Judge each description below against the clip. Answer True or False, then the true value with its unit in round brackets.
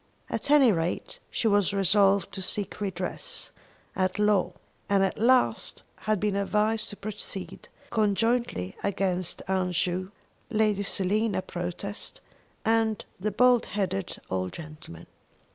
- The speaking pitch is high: True (200 Hz)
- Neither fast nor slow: False (125 wpm)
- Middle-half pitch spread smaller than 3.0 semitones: True (2.6 semitones)